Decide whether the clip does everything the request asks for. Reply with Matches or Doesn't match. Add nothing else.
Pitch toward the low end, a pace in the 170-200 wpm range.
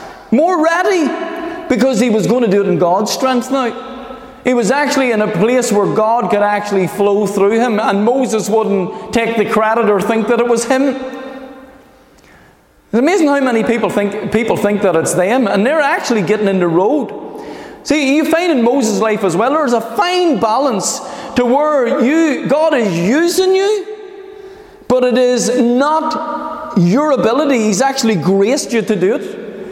Doesn't match